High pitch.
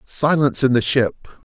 No: low, 135 Hz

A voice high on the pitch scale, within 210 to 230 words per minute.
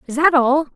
No: very high, 285 Hz; fast, 240 wpm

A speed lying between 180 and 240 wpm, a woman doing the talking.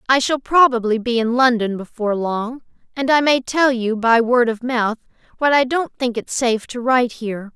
Yes: average, 200 wpm; female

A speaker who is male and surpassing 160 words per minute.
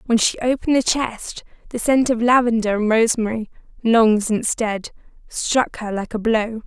No: female; average, 170 wpm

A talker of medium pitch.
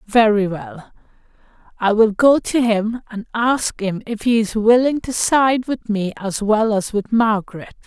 No: high, 220 Hz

